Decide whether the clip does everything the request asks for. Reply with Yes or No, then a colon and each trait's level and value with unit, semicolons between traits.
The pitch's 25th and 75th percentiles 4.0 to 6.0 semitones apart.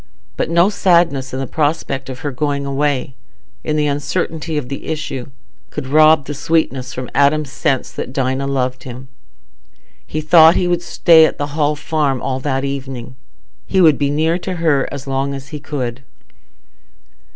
No: average, 2.8 semitones